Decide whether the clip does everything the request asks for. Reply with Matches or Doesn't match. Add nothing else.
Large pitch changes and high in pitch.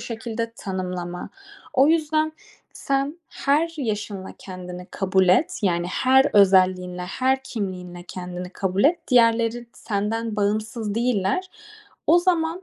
Matches